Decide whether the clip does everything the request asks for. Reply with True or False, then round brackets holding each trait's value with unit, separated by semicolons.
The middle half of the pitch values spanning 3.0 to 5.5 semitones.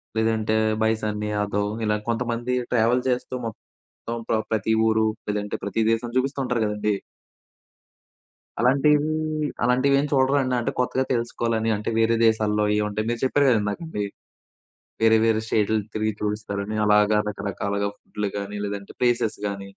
False (2.6 semitones)